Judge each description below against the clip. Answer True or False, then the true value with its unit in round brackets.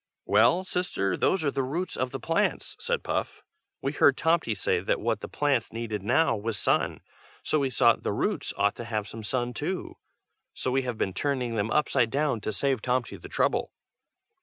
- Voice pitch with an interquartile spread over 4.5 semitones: True (5.1 semitones)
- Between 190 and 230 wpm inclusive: True (200 wpm)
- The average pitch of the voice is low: True (130 Hz)